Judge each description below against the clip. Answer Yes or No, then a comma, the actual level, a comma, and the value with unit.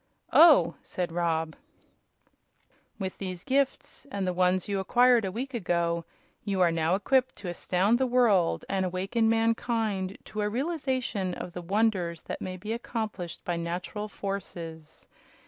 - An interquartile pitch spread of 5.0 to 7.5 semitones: No, average, 4.5 semitones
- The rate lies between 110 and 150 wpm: Yes, average, 145 wpm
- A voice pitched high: Yes, high, 195 Hz